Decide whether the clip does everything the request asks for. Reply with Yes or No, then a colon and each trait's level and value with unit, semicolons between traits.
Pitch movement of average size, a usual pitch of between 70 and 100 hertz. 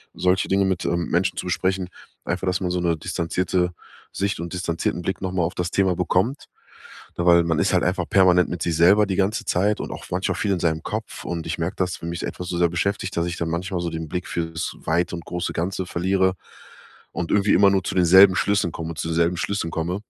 No: narrow, 1.9 semitones; very low, 90 Hz